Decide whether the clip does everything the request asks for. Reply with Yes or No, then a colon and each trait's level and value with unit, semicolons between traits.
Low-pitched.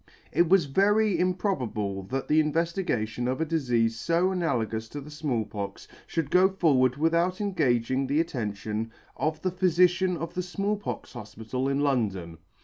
No: medium, 145 Hz